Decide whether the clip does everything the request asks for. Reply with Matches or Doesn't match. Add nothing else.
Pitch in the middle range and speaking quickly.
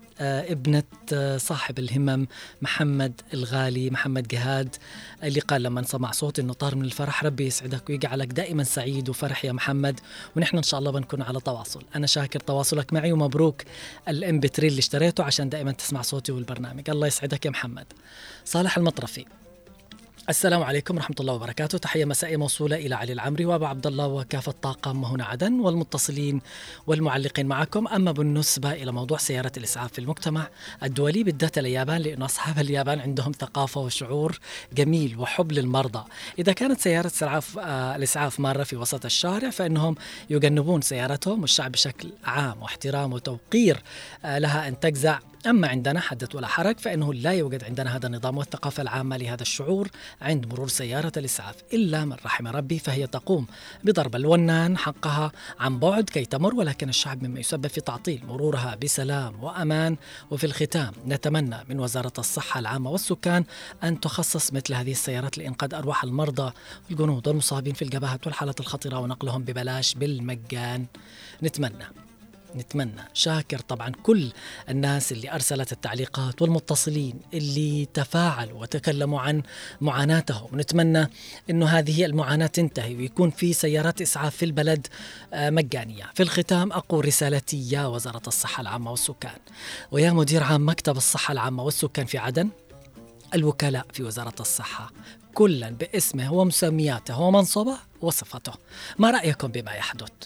Matches